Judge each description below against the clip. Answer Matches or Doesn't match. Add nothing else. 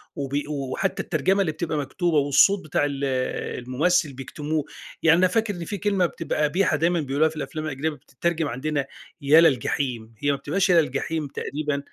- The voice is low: Doesn't match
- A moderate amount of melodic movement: Matches